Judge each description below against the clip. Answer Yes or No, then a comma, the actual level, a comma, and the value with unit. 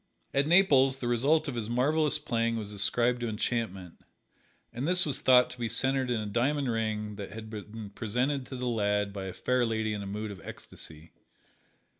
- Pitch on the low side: Yes, low, 115 Hz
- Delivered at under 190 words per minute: No, average, 195 wpm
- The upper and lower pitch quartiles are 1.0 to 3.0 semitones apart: No, average, 3.7 semitones